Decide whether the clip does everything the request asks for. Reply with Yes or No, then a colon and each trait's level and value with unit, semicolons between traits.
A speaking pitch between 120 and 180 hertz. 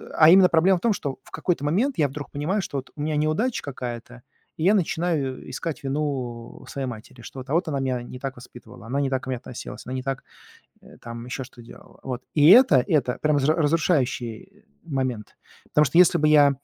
Yes: medium, 140 Hz